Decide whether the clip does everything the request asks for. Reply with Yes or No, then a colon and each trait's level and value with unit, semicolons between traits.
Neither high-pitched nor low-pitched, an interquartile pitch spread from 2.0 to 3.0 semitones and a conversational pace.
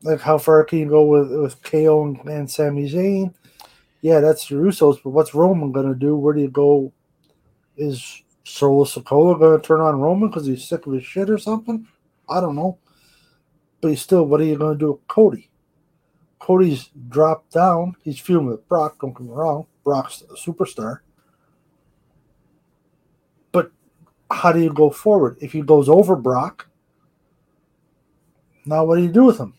Yes: medium, 155 Hz; narrow, 2.5 semitones; average, 180 wpm